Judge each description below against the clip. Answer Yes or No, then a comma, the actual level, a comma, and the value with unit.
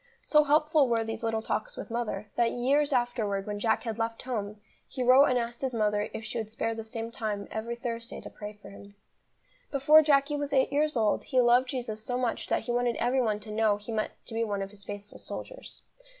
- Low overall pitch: No, high, 230 Hz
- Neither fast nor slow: No, fast, 230 wpm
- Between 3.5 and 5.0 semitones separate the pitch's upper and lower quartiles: No, average, 3.1 semitones